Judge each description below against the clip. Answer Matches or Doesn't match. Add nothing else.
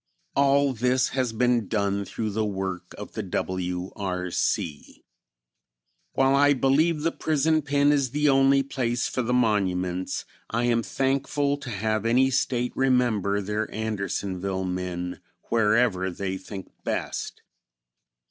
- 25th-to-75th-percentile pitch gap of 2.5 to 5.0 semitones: Doesn't match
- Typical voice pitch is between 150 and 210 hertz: Doesn't match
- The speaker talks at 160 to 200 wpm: Doesn't match